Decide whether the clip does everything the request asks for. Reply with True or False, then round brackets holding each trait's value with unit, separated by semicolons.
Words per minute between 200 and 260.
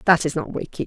False (280 wpm)